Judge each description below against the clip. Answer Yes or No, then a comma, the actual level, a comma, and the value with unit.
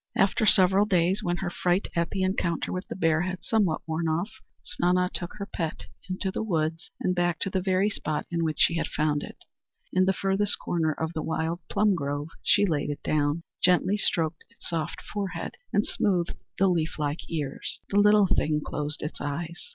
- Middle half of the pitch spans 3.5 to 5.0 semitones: No, average, 3.1 semitones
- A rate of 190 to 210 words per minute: Yes, average, 200 wpm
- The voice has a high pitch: No, medium, 175 Hz